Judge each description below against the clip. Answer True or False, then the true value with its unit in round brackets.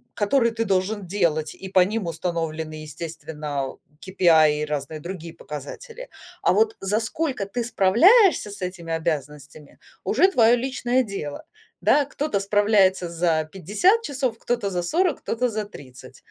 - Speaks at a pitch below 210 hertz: True (190 Hz)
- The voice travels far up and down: True (6.6 semitones)